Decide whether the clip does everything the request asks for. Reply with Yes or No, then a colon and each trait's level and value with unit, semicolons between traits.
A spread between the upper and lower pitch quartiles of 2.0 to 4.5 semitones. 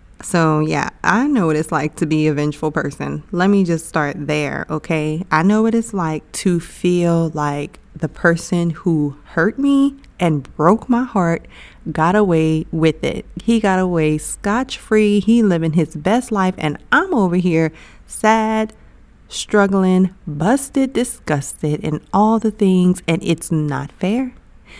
No: average, 5.2 semitones